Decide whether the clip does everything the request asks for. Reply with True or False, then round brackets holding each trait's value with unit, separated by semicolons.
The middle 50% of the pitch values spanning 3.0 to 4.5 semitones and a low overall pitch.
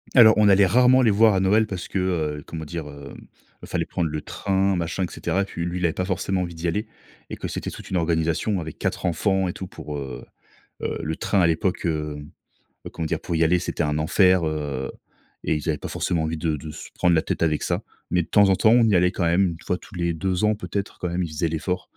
True (3.3 semitones; 85 Hz)